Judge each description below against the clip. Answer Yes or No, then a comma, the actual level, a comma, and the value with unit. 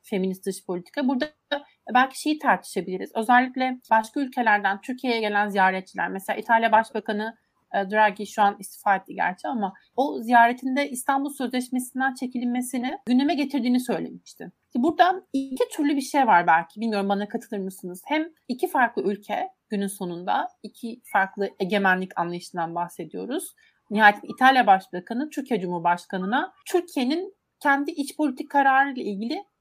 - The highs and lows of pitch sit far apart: Yes, wide, 5.8 semitones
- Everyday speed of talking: Yes, average, 130 wpm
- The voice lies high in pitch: Yes, high, 245 Hz